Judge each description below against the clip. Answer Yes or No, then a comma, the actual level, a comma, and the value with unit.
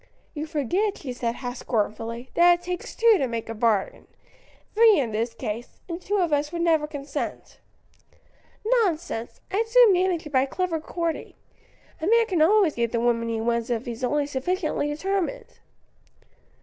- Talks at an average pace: Yes, average, 170 wpm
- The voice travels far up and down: Yes, wide, 7.4 semitones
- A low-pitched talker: No, very high, 300 Hz